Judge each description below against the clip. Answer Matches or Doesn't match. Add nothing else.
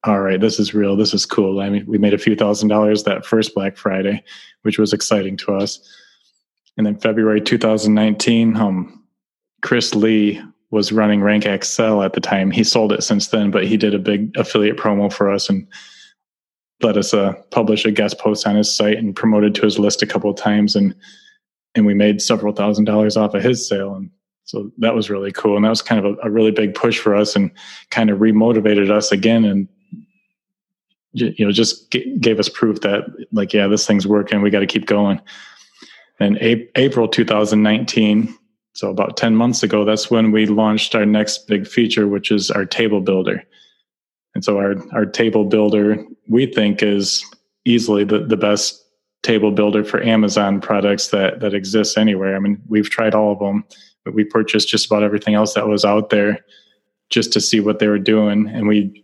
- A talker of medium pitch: Doesn't match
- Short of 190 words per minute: Doesn't match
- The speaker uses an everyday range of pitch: Doesn't match